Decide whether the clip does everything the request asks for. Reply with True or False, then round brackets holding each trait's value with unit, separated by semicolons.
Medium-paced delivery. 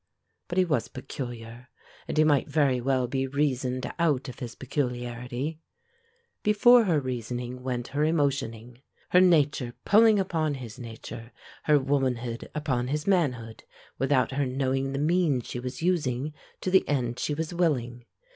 True (150 wpm)